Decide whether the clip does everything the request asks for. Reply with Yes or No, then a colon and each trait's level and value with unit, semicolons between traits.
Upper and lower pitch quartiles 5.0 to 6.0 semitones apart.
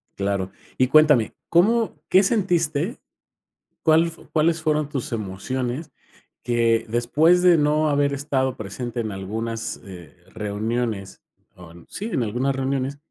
Yes: wide, 5.6 semitones